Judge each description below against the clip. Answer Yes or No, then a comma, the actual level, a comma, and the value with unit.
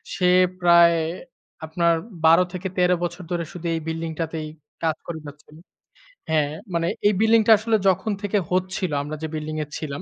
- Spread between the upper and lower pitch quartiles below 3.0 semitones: Yes, narrow, 2.5 semitones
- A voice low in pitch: No, medium, 170 Hz